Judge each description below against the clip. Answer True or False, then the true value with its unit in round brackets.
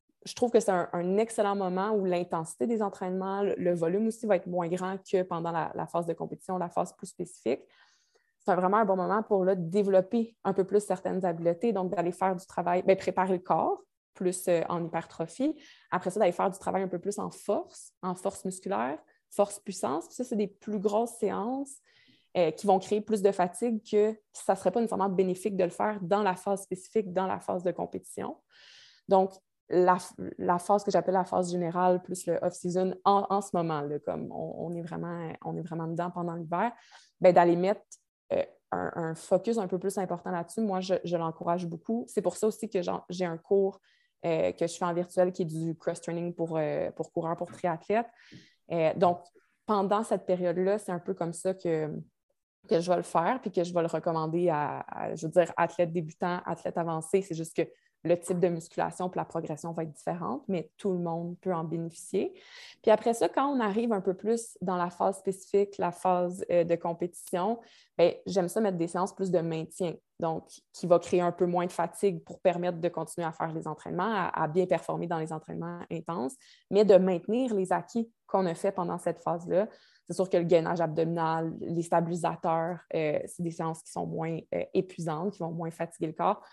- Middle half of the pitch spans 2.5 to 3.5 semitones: True (2.8 semitones)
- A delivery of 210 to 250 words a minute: True (215 wpm)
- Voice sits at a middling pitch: True (180 Hz)